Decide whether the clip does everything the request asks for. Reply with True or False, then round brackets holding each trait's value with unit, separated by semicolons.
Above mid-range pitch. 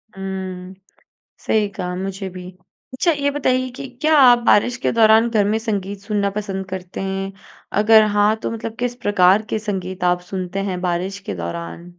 True (195 Hz)